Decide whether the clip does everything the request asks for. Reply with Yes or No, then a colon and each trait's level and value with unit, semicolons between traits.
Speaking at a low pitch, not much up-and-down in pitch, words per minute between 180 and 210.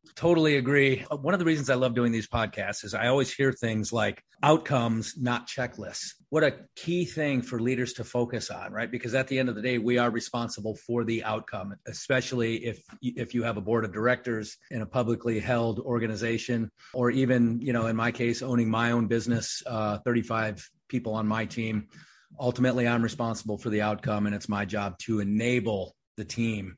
Yes: low, 120 Hz; narrow, 2.2 semitones; average, 195 wpm